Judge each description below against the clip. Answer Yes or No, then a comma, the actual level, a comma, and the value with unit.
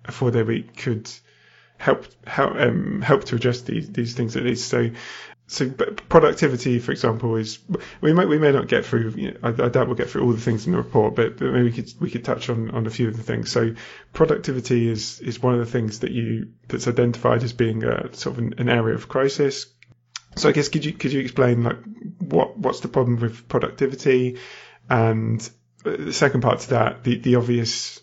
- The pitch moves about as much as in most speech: No, narrow, 2.3 semitones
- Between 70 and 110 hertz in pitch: No, low, 120 Hz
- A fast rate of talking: Yes, fast, 220 wpm